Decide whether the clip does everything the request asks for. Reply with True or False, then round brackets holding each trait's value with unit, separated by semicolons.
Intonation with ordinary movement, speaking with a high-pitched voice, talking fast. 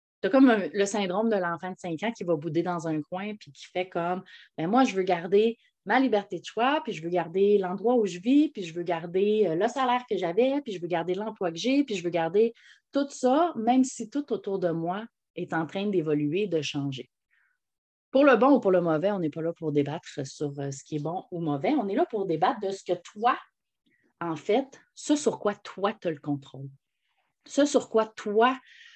False (6.0 semitones; 195 Hz; 230 wpm)